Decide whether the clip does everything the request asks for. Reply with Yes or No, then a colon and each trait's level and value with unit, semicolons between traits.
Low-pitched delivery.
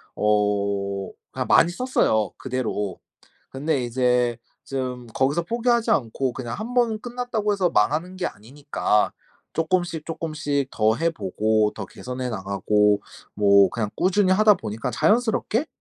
Yes: low, 130 Hz